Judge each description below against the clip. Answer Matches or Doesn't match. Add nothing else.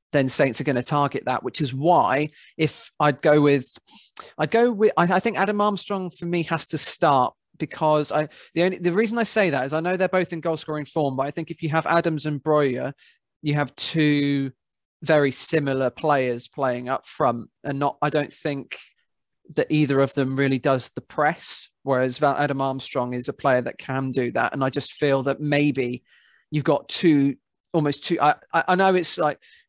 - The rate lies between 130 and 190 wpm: Doesn't match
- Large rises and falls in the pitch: Doesn't match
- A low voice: Doesn't match